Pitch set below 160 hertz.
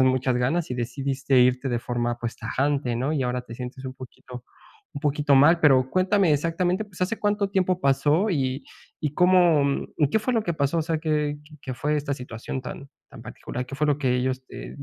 Yes: medium, 140 Hz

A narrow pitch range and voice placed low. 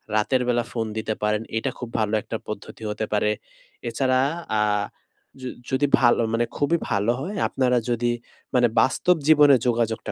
No: average, 3.0 semitones; low, 120 Hz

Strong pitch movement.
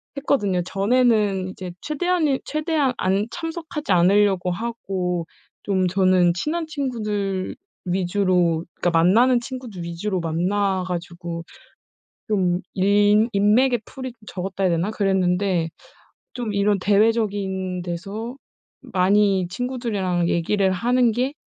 No: average, 4.5 semitones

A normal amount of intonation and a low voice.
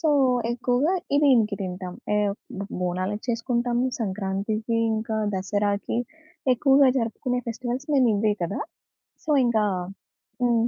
No: average, 3.4 semitones; high, 225 Hz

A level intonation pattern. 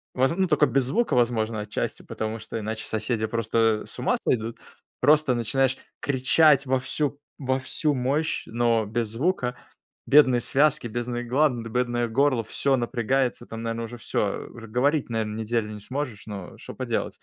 No: average, 3.1 semitones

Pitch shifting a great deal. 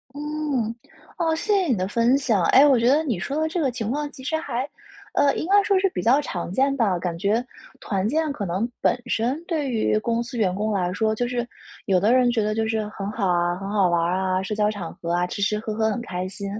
Yes: wide, 5.8 semitones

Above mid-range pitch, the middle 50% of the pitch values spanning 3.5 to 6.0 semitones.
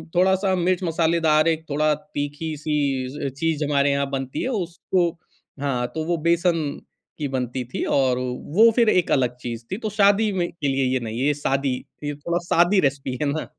No: medium, 150 Hz; average, 4.1 semitones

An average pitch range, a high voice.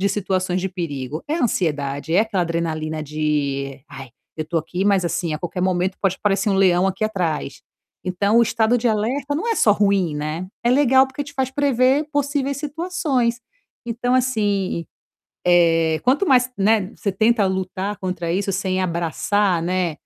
No: wide, 5.9 semitones; high, 195 Hz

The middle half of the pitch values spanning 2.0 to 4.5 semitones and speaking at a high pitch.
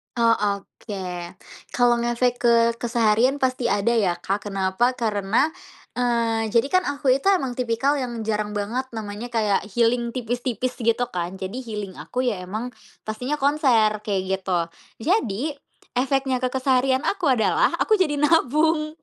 Yes: average, 3.5 semitones; high, 240 Hz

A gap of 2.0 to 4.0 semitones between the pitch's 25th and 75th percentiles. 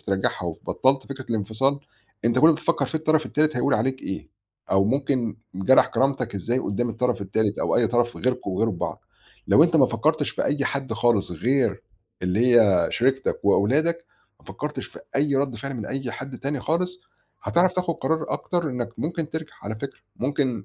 No: average, 4.9 semitones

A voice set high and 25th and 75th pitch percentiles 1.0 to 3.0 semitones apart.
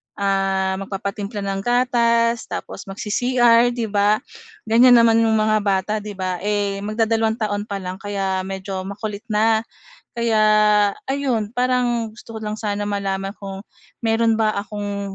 Yes: high, 210 Hz; narrow, 2.5 semitones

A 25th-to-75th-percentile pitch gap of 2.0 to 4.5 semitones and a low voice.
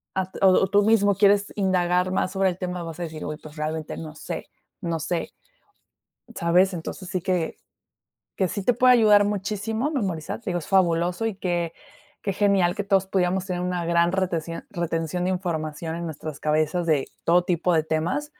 No: average, 2.8 semitones; medium, 180 Hz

